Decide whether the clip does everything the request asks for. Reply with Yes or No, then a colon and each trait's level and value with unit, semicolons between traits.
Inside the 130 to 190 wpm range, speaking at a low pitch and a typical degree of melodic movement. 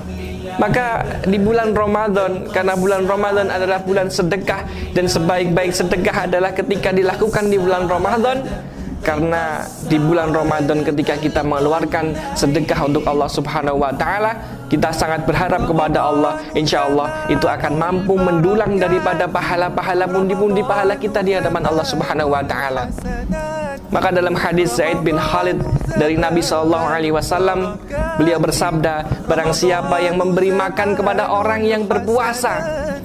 No: fast, 140 wpm; medium, 180 Hz; average, 3.9 semitones